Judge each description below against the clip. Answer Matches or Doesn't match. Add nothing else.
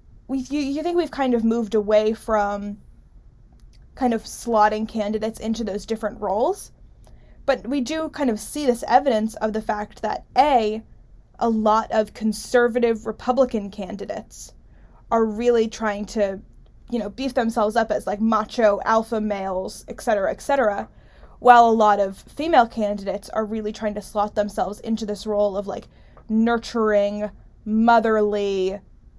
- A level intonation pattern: Matches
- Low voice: Doesn't match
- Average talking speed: Matches